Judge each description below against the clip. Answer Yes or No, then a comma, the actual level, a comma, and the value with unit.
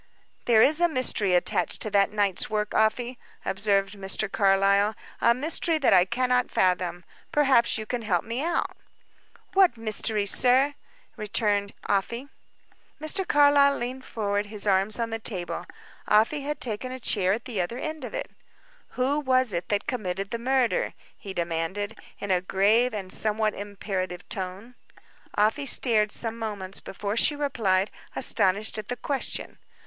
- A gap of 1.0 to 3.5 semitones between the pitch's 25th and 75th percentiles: No, average, 4.2 semitones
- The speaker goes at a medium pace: Yes, average, 155 wpm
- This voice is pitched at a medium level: No, high, 215 Hz